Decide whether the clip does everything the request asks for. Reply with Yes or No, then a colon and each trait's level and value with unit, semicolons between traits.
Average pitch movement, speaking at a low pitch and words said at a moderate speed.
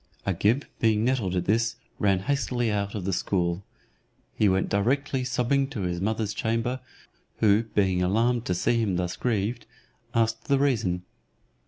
Yes: average, 3.9 semitones; low, 110 Hz; average, 155 wpm